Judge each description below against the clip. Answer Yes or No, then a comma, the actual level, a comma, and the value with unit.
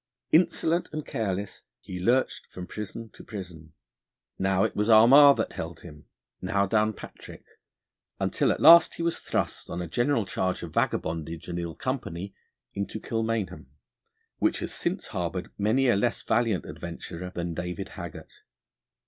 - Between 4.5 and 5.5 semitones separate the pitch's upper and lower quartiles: Yes, average, 4.9 semitones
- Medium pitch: No, low, 100 Hz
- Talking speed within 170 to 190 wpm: No, average, 150 wpm